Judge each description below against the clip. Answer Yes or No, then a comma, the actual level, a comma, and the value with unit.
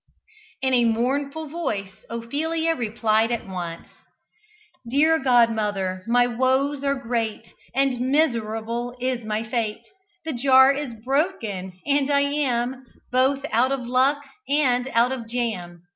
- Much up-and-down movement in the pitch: No, average, 3.6 semitones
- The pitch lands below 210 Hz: No, high, 245 Hz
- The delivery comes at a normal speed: No, slow, 130 wpm